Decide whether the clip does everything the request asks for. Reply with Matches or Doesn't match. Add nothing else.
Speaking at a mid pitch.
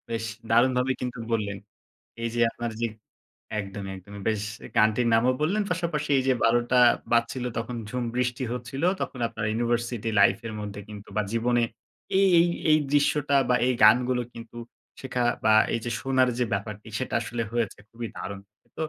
Doesn't match